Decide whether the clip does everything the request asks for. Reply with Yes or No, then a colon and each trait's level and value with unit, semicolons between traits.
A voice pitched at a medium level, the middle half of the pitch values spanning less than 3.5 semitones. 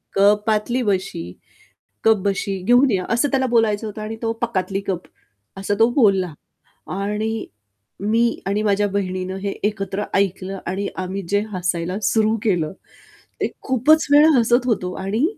No: high, 205 Hz; average, 2.8 semitones